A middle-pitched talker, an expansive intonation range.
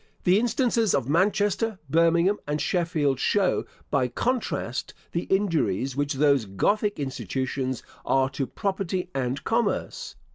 Yes: medium, 165 Hz; wide, 6.9 semitones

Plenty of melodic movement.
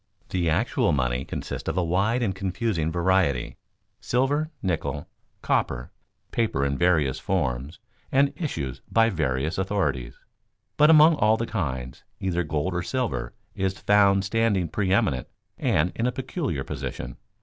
Yes: wide, 7.8 semitones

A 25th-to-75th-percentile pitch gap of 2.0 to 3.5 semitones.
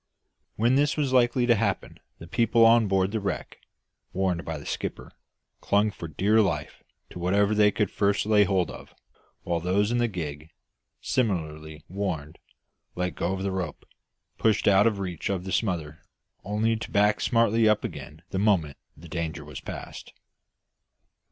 No: average, 4.3 semitones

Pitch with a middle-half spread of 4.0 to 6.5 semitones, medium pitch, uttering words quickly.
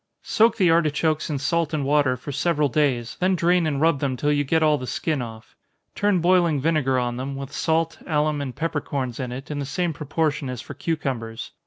No: average, 3.6 semitones; medium, 150 Hz; fast, 215 wpm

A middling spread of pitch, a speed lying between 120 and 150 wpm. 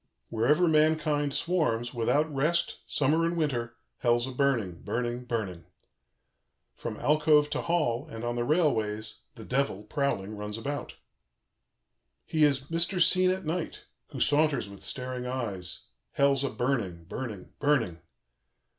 Yes: average, 5.0 semitones; slow, 135 wpm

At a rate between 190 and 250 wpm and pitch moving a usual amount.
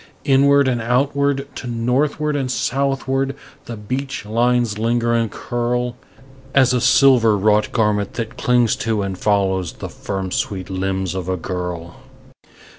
No: average, 140 wpm; average, 4.5 semitones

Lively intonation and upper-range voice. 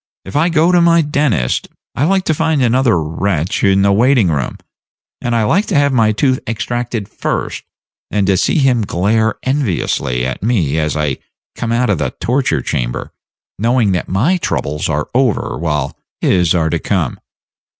No: wide, 7.8 semitones; low, 110 Hz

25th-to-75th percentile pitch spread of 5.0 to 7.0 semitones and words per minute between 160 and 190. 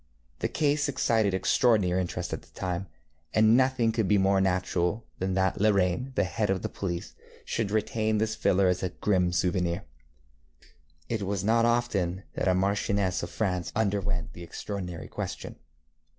No: average, 3.2 semitones; average, 165 wpm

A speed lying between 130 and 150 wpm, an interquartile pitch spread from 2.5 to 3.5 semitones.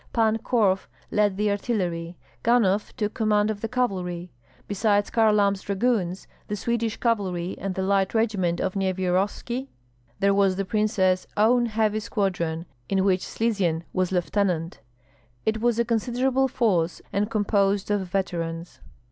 Yes: average, 140 wpm; average, 2.9 semitones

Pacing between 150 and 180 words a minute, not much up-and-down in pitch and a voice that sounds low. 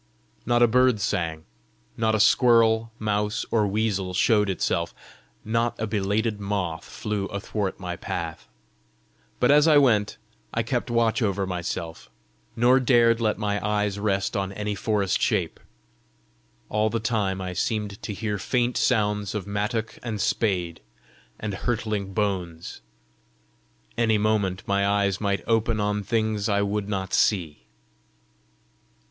No: average, 140 wpm; narrow, 2.3 semitones; low, 105 Hz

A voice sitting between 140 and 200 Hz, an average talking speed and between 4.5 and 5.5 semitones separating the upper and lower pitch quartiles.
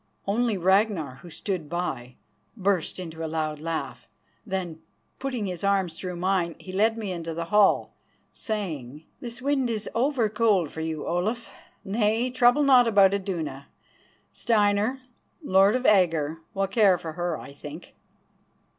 Yes: high, 190 Hz; average, 145 wpm; average, 5.0 semitones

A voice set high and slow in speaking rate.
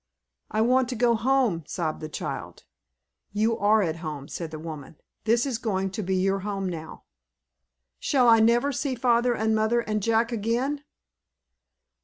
No: high, 220 Hz; average, 165 wpm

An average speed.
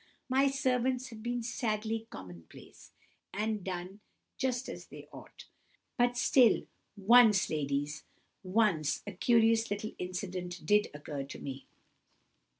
No: slow, 120 wpm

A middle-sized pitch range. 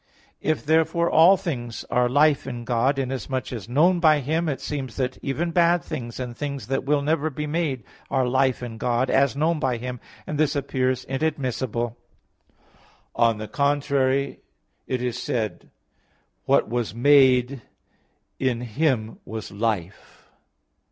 Yes: average, 3.5 semitones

